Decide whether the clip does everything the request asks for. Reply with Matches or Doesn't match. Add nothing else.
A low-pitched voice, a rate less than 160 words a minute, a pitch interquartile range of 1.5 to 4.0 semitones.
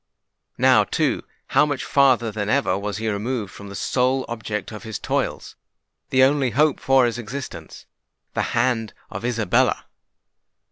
Matches